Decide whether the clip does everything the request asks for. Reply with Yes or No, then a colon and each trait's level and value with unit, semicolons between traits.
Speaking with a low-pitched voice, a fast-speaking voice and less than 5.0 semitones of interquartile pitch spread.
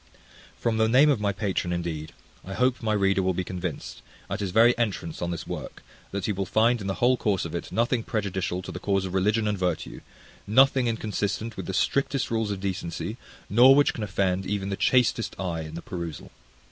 Yes: low, 100 Hz; fast, 210 wpm; average, 3.7 semitones